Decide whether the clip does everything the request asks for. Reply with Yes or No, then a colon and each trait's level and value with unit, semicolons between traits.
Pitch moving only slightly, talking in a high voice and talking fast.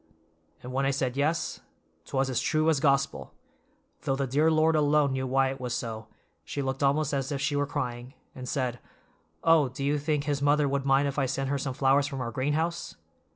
No: narrow, 1.8 semitones; medium, 140 Hz; fast, 215 wpm